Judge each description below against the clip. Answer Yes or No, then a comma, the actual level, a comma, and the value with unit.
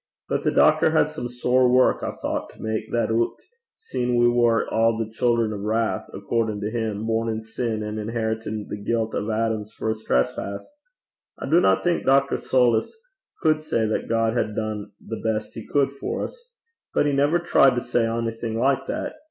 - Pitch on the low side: Yes, low, 115 Hz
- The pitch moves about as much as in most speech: No, narrow, 2.1 semitones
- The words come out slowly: No, average, 190 wpm